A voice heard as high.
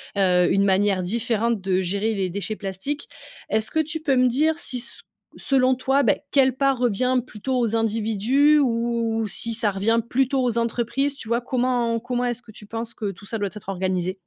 Yes: high, 230 Hz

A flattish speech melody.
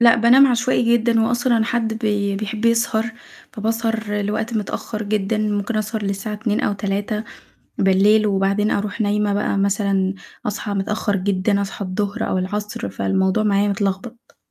Yes: narrow, 2.0 semitones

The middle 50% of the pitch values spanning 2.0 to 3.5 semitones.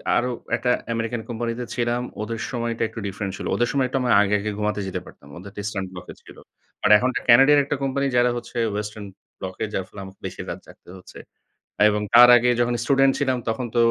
Yes: average, 2.9 semitones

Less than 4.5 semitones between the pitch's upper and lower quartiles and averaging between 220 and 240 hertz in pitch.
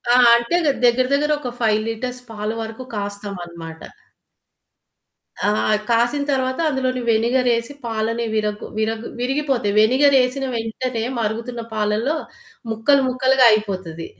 Yes: average, 3.1 semitones; high, 235 Hz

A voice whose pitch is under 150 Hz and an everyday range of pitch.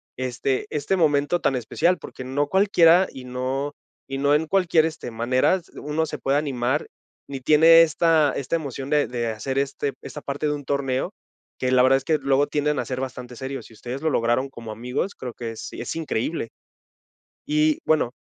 Yes: medium, 140 Hz; average, 3.3 semitones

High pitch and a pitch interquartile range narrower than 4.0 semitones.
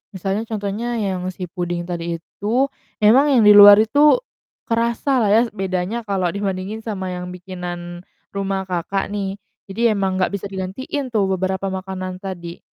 Yes: high, 195 Hz; average, 2.7 semitones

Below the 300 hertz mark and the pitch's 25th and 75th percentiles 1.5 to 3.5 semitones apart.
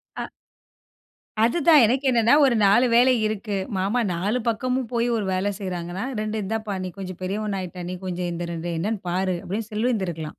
No: high, 205 Hz; average, 4.2 semitones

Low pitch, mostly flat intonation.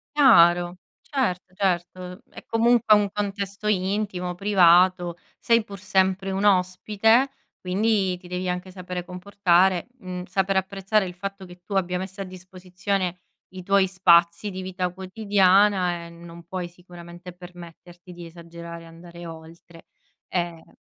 No: medium, 185 Hz; narrow, 2.0 semitones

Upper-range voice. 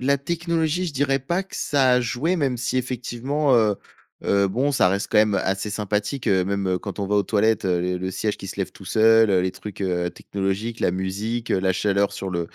No: low, 105 Hz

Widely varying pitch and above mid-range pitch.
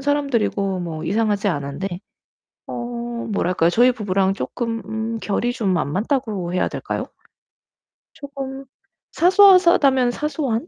Yes: wide, 6.1 semitones; high, 225 Hz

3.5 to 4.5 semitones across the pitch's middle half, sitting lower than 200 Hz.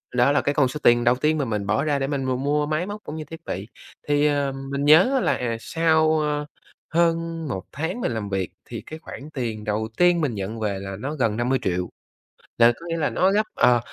No: average, 5.2 semitones; medium, 140 Hz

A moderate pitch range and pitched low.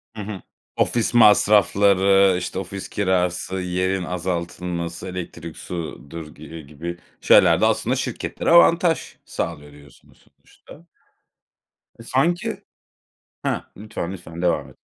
Yes: average, 3.0 semitones; very low, 90 Hz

